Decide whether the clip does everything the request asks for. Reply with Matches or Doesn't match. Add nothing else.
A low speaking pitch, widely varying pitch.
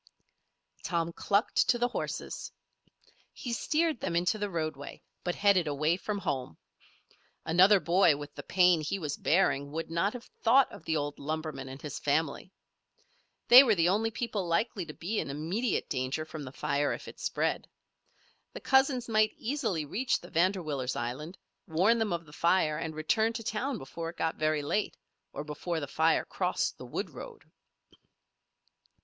Doesn't match